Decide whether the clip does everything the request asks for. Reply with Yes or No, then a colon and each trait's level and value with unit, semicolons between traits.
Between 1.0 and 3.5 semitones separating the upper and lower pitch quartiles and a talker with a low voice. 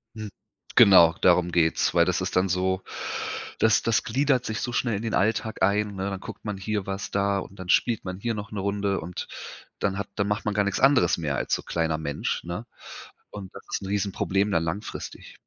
Yes: narrow, 2.4 semitones; low, 100 Hz